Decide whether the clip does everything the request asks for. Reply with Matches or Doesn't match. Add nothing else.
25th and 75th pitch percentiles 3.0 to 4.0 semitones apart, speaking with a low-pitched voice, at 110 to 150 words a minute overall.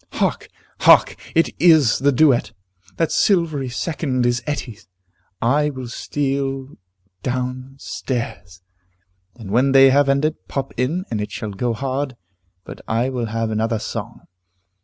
Matches